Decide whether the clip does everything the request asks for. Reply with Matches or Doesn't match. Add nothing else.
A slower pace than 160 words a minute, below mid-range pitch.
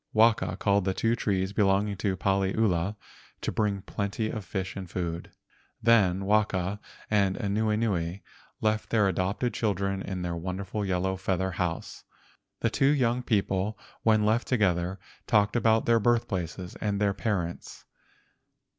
Matches